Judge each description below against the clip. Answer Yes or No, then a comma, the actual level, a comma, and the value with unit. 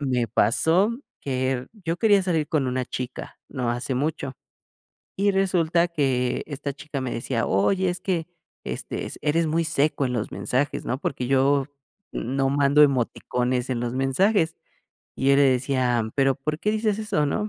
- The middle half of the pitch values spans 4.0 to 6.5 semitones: Yes, average, 4.5 semitones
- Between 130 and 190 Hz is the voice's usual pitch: Yes, medium, 140 Hz